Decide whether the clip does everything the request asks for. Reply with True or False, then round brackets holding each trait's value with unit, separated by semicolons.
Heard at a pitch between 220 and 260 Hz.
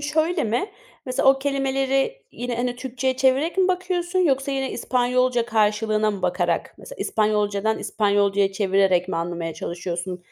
True (240 Hz)